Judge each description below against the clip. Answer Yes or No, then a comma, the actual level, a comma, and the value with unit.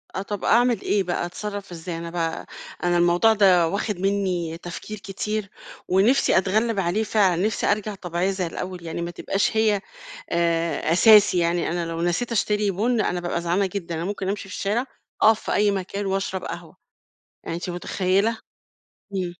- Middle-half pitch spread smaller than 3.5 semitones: Yes, average, 3.0 semitones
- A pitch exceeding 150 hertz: Yes, high, 190 Hz